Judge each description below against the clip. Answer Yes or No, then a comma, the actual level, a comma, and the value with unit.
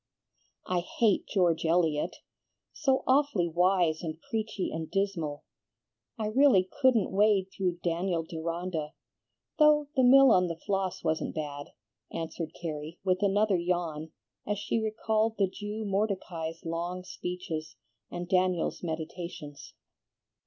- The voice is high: No, medium, 180 Hz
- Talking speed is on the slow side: Yes, slow, 125 wpm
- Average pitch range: Yes, average, 4.0 semitones